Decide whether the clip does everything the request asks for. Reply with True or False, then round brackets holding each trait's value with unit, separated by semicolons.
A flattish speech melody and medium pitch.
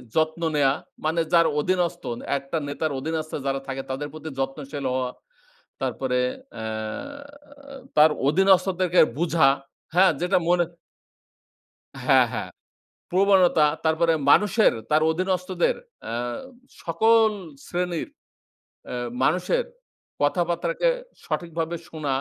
False (3.9 semitones; 165 Hz)